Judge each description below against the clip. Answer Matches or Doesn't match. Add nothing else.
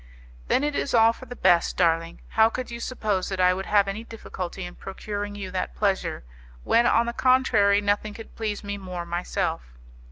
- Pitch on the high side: Matches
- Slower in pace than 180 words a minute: Doesn't match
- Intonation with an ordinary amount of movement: Matches